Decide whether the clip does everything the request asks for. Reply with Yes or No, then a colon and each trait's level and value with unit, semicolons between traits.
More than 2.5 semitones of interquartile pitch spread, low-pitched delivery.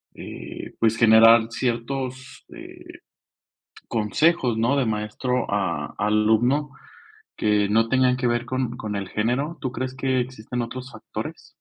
Yes: average, 2.9 semitones; low, 120 Hz